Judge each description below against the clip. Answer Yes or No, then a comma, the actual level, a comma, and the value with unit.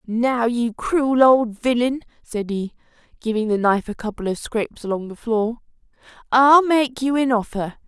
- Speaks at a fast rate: No, average, 170 wpm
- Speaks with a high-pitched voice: Yes, high, 235 Hz